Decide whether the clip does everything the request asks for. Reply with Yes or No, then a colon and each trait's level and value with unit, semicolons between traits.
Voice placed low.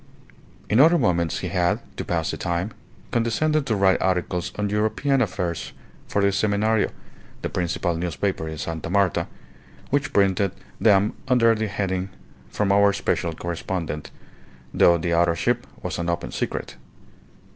Yes: very low, 95 Hz